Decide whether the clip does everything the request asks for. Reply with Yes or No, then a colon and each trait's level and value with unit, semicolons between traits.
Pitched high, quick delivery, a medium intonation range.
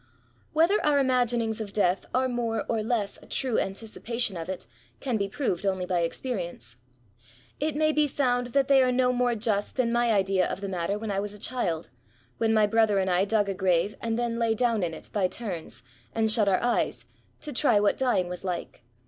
Yes: high, 220 Hz; fast, 210 wpm; average, 4.2 semitones